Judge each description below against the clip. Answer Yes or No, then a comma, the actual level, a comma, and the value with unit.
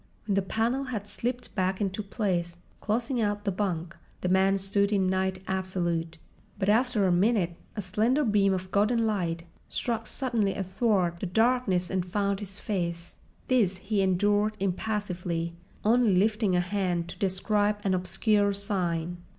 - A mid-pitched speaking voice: No, high, 195 Hz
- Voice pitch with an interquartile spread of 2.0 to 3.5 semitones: Yes, average, 2.7 semitones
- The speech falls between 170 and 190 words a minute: No, average, 155 wpm